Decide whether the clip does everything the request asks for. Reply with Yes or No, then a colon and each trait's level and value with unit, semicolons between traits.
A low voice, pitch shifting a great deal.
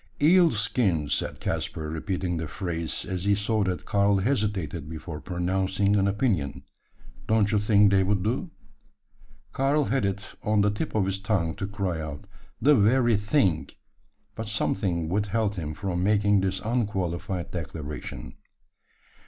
No: low, 100 Hz; average, 3.3 semitones